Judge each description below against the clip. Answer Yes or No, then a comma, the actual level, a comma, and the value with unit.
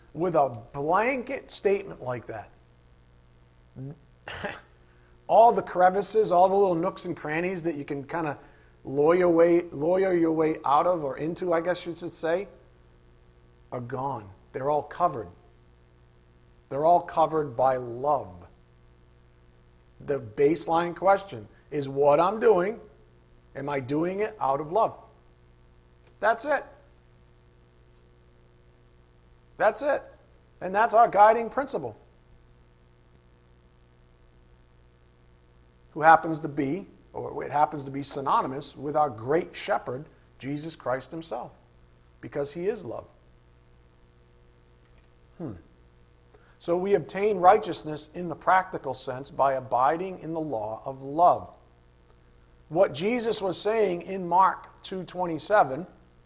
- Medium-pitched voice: No, low, 125 Hz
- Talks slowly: Yes, slow, 115 wpm